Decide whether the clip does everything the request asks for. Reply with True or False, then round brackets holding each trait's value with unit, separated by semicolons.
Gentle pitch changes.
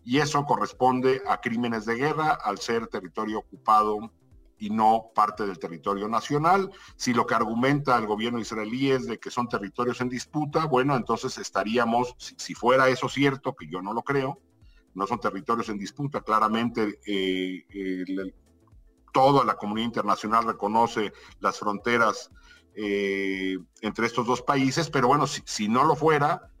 False (3.9 semitones)